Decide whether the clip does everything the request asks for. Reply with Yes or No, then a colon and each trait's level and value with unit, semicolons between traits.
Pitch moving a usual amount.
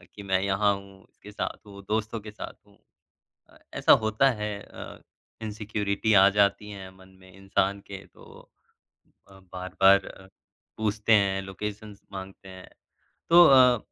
No: narrow, 1.6 semitones